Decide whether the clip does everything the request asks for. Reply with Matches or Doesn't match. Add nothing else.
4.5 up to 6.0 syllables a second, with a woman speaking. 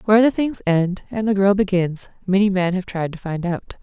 Matches